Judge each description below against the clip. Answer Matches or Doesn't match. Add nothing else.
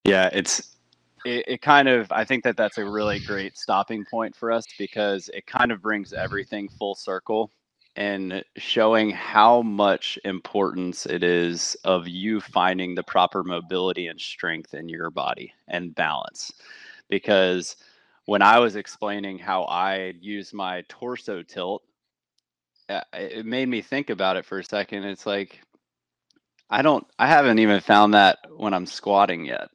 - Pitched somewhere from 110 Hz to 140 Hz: Doesn't match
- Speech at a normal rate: Matches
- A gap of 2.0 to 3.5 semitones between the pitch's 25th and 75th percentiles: Matches